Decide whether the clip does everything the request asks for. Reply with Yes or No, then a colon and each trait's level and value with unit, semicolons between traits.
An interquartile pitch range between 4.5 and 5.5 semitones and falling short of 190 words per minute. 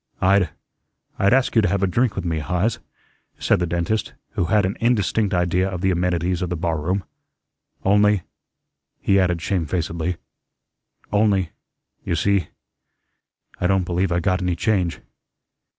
No: narrow, 2.4 semitones; average, 150 wpm